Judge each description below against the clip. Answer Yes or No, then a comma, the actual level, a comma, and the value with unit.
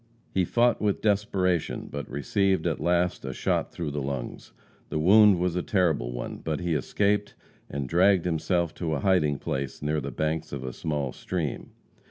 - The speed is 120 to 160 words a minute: No, average, 180 wpm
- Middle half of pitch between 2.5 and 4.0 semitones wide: No, average, 4.6 semitones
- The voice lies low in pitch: Yes, very low, 85 Hz